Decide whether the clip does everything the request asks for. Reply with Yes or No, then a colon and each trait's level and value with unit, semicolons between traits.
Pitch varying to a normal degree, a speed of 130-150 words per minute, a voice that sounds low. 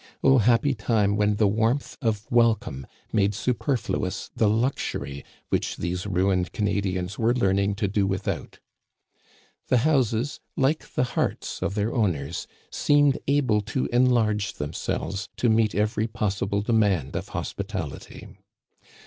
Yes: average, 3.4 semitones; slow, 135 wpm; low, 105 Hz